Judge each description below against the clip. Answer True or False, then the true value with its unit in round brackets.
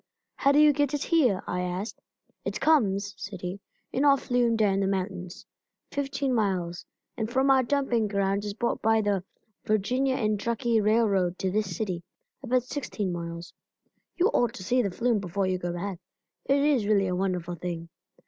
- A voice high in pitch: True (210 Hz)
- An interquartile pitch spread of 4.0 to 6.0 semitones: True (5.2 semitones)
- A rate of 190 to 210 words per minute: False (180 wpm)